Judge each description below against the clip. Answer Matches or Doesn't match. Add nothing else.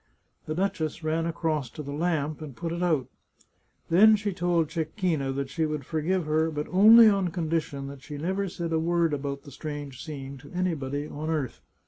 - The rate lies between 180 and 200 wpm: Matches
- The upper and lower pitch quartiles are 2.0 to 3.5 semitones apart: Matches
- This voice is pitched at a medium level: Matches